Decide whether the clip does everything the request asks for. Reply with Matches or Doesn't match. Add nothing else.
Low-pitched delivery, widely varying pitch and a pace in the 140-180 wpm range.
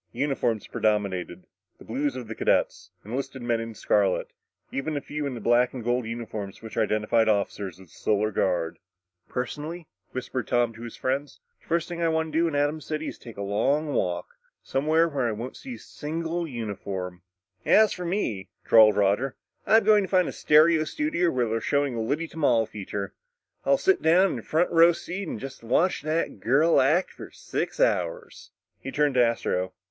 Doesn't match